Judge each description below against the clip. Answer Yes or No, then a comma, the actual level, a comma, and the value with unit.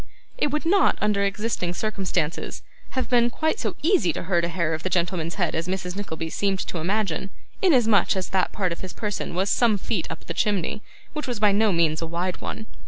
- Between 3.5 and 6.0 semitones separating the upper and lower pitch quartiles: Yes, average, 4.1 semitones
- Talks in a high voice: Yes, high, 195 Hz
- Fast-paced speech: Yes, fast, 215 wpm